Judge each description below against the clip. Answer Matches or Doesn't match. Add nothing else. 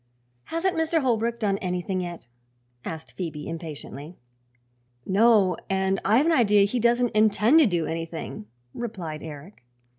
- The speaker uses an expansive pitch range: Matches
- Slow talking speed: Matches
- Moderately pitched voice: Doesn't match